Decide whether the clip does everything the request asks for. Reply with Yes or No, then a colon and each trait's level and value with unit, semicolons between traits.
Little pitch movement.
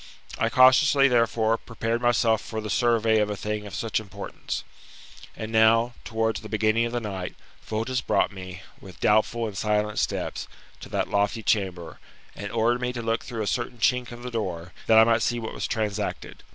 Yes: narrow, 2.0 semitones